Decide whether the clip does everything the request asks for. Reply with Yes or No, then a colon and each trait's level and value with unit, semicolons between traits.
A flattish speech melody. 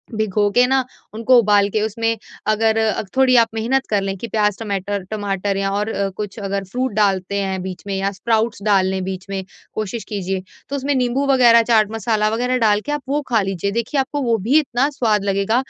No: average, 3.0 semitones